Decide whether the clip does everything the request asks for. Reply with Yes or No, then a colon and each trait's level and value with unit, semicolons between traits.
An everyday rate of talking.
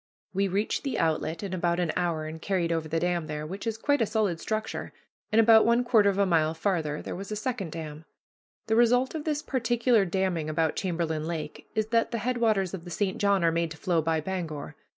No: fast, 225 wpm